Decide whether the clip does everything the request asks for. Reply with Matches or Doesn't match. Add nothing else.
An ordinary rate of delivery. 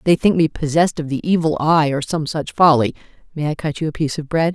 Doesn't match